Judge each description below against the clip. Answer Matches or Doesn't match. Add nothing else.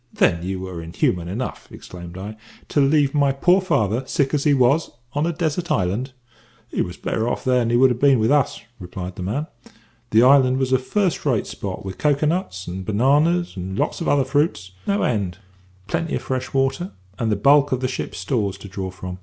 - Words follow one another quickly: Matches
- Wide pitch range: Matches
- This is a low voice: Matches